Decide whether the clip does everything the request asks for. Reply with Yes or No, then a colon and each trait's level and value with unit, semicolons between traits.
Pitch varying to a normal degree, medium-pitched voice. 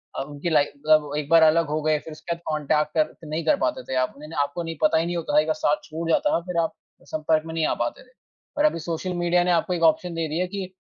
No: narrow, 2.0 semitones; medium, 160 Hz